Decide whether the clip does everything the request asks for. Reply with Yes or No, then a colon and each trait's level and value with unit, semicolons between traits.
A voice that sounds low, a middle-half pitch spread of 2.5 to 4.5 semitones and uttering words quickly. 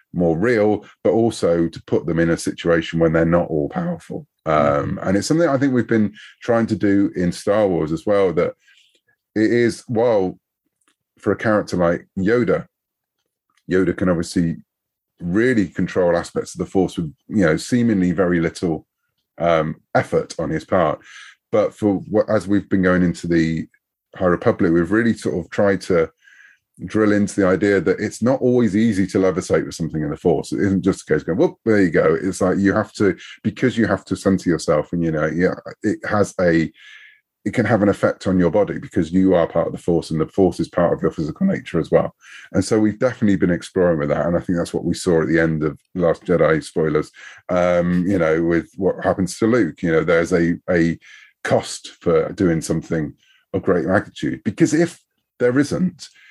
Yes: very low, 95 Hz; average, 4.2 semitones; fast, 210 wpm